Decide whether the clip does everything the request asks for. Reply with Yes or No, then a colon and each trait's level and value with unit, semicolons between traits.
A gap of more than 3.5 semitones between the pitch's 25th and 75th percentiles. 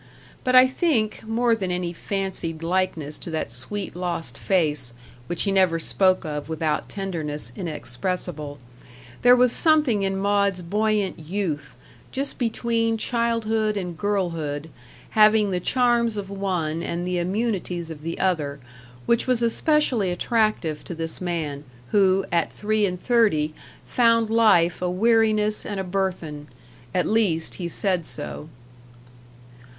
Yes: average, 4.7 semitones